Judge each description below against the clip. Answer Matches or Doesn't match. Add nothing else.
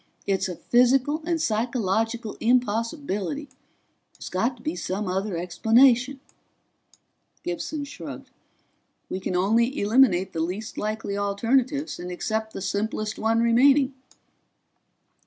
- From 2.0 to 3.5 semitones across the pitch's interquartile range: Doesn't match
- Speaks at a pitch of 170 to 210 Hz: Doesn't match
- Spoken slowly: Matches